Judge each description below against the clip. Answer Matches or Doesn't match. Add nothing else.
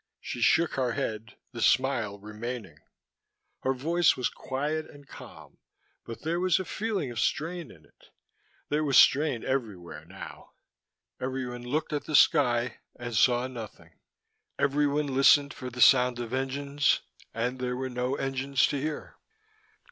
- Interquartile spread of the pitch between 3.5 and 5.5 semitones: Doesn't match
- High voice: Doesn't match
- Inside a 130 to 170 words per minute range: Matches